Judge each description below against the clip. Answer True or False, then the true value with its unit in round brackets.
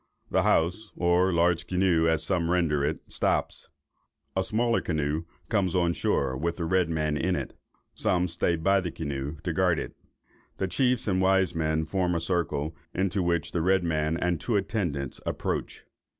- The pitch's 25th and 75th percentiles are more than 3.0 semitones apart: False (2.7 semitones)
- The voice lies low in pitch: True (85 Hz)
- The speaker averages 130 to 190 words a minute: True (175 wpm)